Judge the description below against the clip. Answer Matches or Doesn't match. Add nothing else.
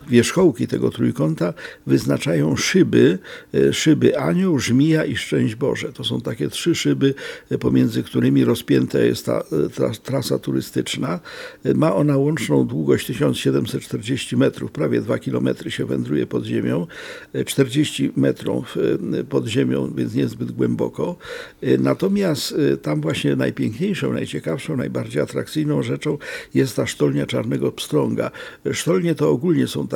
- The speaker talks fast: Doesn't match